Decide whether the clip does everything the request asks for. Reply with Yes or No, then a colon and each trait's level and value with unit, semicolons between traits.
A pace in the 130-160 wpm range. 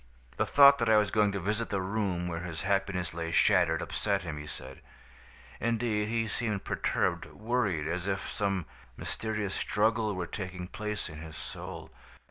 No: average, 170 wpm